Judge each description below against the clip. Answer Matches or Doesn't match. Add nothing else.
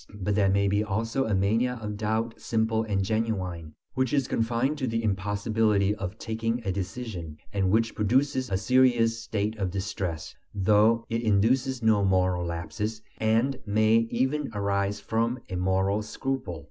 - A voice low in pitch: Matches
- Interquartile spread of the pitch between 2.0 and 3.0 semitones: Matches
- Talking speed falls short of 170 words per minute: Matches